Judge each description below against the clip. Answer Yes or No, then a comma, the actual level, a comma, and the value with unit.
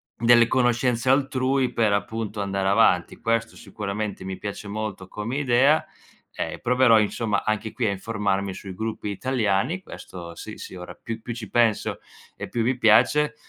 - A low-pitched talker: Yes, low, 110 Hz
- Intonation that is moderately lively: Yes, average, 3.3 semitones